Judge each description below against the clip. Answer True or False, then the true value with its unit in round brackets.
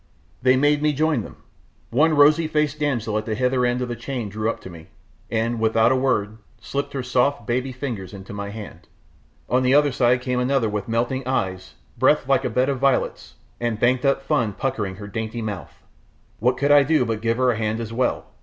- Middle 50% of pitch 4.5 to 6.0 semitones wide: False (3.5 semitones)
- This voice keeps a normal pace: False (215 wpm)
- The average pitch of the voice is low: True (125 Hz)